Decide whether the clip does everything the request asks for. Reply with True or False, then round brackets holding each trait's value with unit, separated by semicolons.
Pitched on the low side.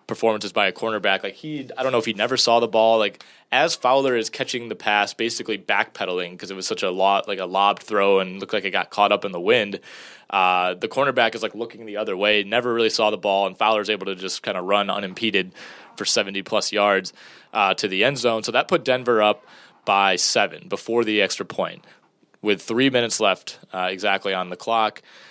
True (105 Hz)